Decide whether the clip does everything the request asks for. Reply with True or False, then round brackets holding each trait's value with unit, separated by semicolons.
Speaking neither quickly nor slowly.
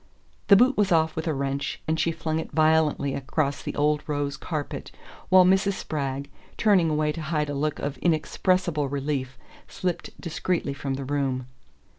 True (170 wpm)